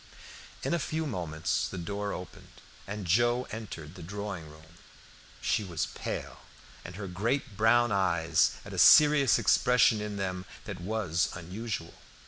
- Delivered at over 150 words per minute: No, average, 145 wpm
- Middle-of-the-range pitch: No, low, 100 Hz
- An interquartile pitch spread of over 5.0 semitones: No, average, 4.6 semitones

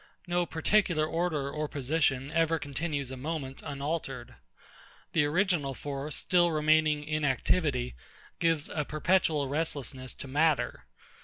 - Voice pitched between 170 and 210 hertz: No, medium, 150 Hz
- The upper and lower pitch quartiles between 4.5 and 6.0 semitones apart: No, average, 2.8 semitones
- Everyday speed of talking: No, slow, 125 wpm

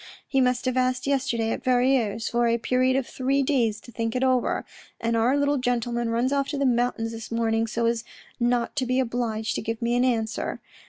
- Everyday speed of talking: No, fast, 215 wpm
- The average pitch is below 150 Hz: No, high, 245 Hz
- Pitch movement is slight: Yes, narrow, 2.0 semitones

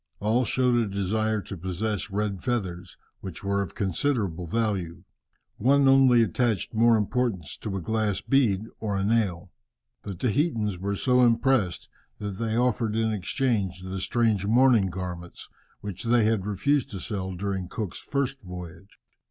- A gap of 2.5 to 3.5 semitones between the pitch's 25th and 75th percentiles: No, average, 3.9 semitones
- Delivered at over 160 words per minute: No, average, 150 wpm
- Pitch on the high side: No, low, 105 Hz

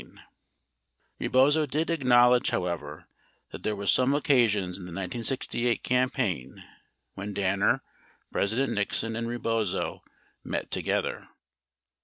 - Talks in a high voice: No, low, 115 Hz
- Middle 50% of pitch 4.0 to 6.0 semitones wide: Yes, average, 4.6 semitones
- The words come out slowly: Yes, slow, 110 wpm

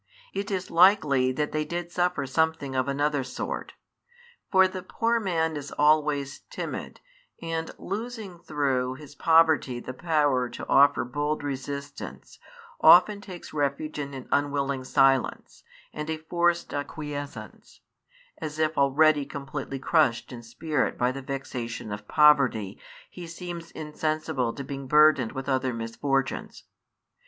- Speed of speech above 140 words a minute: No, slow, 135 wpm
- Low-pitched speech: No, medium, 145 Hz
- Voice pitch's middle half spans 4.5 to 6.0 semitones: No, average, 3.2 semitones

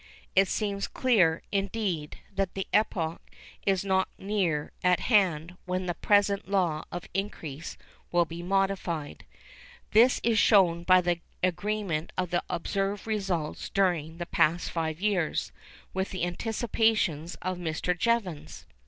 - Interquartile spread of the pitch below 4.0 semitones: Yes, average, 2.9 semitones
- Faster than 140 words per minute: No, slow, 135 wpm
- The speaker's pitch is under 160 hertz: No, medium, 185 Hz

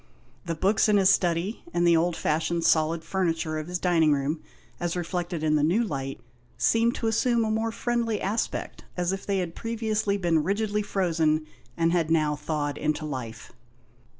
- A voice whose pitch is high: No, medium, 175 Hz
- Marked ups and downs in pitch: No, average, 4.4 semitones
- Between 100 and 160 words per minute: No, average, 180 wpm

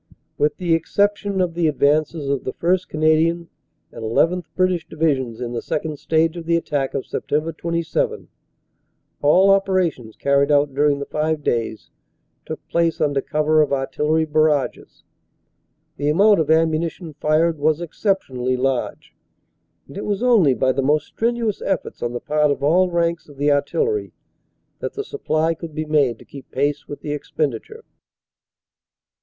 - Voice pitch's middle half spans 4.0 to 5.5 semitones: No, average, 3.0 semitones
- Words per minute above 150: Yes, average, 160 wpm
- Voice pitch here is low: No, medium, 155 Hz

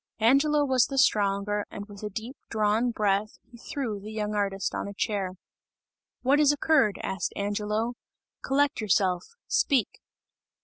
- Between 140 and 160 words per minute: Yes, average, 145 wpm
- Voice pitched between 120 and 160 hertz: No, high, 215 Hz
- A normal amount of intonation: Yes, average, 4.4 semitones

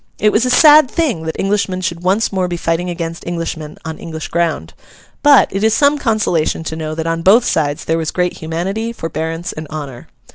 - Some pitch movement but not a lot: Yes, average, 4.6 semitones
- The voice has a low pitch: No, medium, 170 Hz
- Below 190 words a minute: No, fast, 205 wpm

